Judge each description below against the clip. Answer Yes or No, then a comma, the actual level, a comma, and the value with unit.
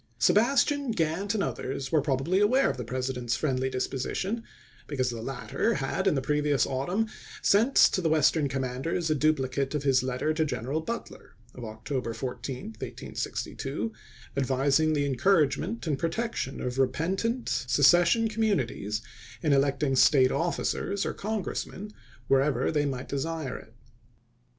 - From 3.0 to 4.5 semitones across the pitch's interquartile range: No, average, 5.2 semitones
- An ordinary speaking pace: Yes, average, 145 wpm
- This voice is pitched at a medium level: Yes, medium, 145 Hz